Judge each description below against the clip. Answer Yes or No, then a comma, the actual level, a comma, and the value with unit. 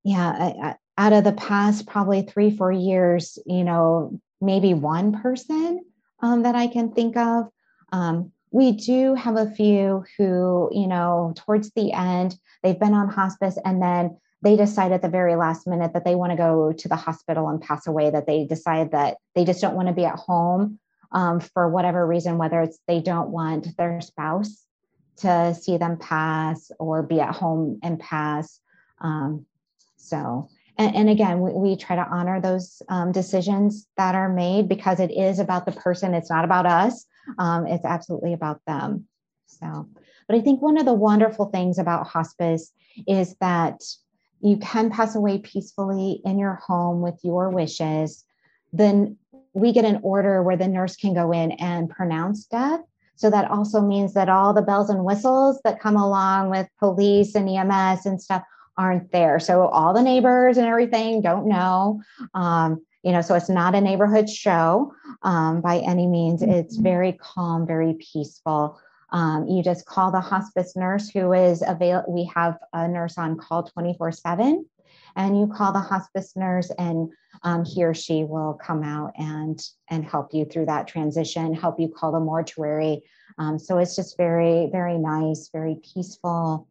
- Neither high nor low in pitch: Yes, medium, 180 Hz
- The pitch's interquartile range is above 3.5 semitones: No, average, 3.2 semitones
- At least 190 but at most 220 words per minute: No, average, 180 wpm